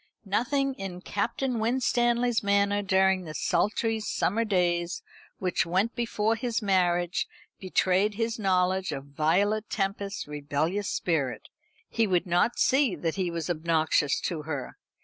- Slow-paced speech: Yes, slow, 130 wpm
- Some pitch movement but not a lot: Yes, average, 4.2 semitones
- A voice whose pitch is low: No, high, 190 Hz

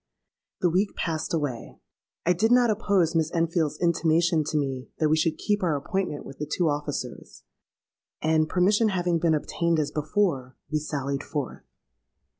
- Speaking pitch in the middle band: Yes, medium, 160 Hz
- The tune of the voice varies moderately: Yes, average, 3.1 semitones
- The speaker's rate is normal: Yes, average, 160 wpm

